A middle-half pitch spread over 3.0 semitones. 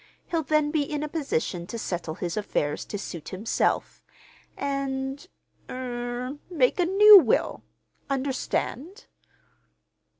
Yes: average, 5.1 semitones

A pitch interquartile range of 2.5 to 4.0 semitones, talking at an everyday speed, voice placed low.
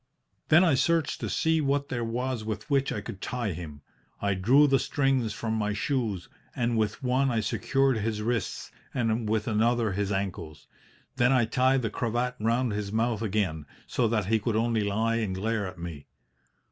Yes: average, 3.4 semitones; average, 185 wpm; low, 115 Hz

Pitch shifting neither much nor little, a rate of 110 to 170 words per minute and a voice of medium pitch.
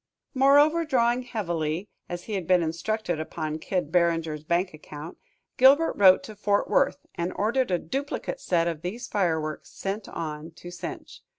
No: wide, 5.9 semitones; average, 160 wpm; medium, 180 Hz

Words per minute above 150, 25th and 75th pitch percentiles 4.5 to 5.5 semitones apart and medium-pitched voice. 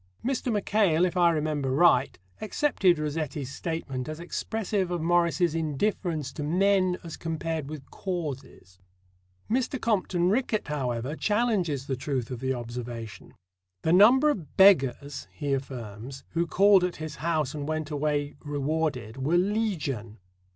No: slow, 135 wpm; average, 5.0 semitones; medium, 155 Hz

